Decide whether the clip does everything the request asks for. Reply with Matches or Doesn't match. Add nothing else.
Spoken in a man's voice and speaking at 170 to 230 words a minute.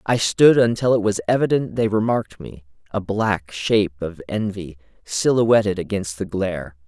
Doesn't match